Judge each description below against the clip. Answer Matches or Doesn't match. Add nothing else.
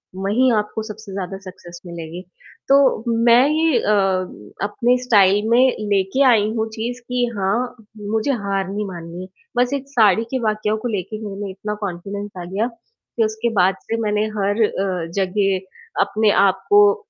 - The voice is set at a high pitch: Matches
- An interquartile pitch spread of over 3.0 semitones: Matches